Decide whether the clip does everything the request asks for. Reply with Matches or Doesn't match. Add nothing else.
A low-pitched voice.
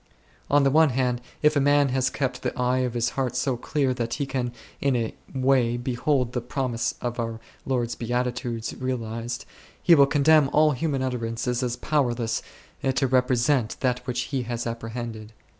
Matches